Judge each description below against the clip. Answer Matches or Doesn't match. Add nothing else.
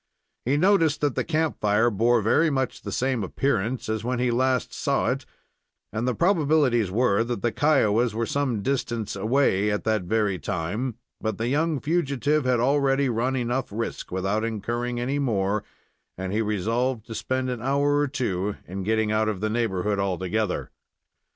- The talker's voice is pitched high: Doesn't match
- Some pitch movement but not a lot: Matches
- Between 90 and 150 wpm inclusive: Doesn't match